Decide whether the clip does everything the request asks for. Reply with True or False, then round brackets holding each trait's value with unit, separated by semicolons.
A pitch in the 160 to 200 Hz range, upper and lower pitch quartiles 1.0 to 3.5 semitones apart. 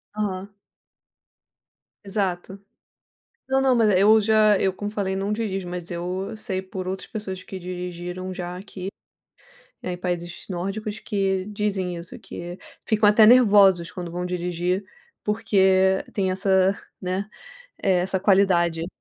True (190 Hz; 2.4 semitones)